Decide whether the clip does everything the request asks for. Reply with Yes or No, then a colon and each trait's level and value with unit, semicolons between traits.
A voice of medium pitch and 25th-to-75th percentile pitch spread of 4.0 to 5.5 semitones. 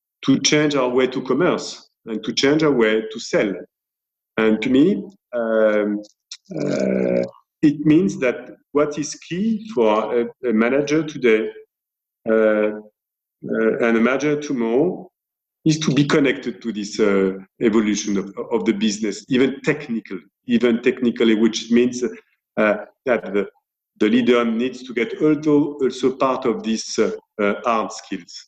No: low, 120 Hz; average, 5.1 semitones